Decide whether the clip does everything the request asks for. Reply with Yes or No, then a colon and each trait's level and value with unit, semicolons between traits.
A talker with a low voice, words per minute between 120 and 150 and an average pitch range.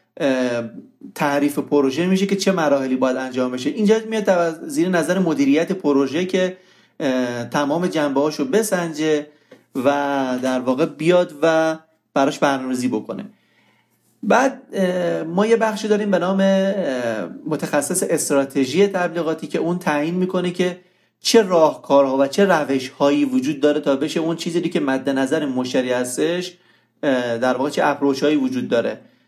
No: medium, 160 Hz; average, 125 wpm; average, 4.8 semitones